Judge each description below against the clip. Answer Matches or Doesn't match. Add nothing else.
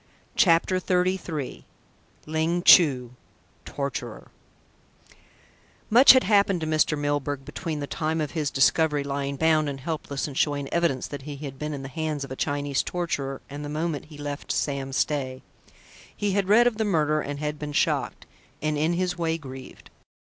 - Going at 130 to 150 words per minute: Doesn't match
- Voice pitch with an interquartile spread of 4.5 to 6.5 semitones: Doesn't match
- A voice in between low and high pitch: Matches